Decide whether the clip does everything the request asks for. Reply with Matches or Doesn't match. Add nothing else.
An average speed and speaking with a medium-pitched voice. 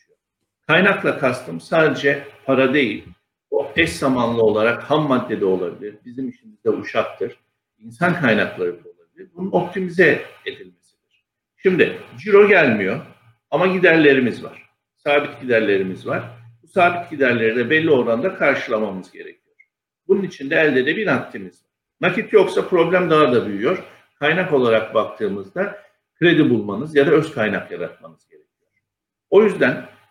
Matches